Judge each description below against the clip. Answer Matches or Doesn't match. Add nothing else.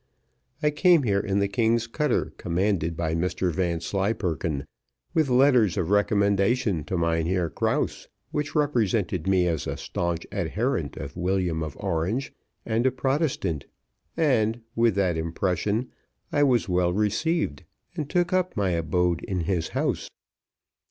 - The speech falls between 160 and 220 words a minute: Doesn't match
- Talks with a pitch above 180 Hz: Doesn't match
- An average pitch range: Doesn't match